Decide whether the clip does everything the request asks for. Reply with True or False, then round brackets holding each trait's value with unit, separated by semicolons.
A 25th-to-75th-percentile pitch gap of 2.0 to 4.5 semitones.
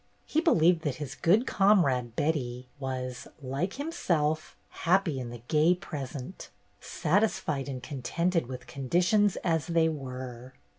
False (5.4 semitones)